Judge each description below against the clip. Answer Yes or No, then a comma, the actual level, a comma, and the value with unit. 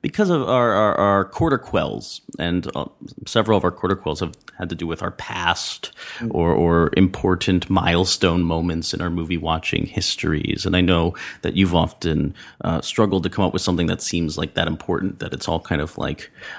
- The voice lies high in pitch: No, very low, 90 Hz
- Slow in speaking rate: No, fast, 205 wpm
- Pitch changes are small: Yes, narrow, 2.3 semitones